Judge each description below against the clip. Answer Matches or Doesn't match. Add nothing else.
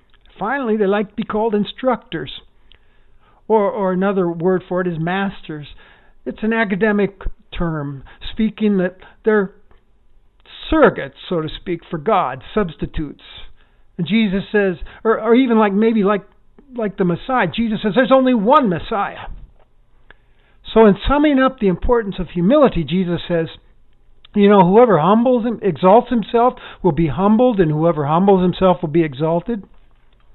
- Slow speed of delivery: Doesn't match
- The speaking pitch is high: Matches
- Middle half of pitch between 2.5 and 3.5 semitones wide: Doesn't match